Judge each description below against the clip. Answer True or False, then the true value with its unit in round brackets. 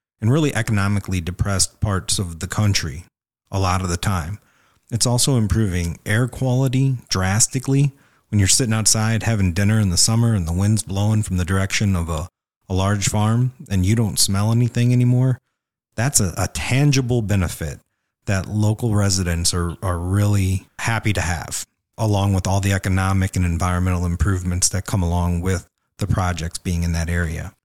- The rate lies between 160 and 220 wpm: True (170 wpm)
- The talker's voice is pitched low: True (100 Hz)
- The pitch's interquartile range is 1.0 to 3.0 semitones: False (3.7 semitones)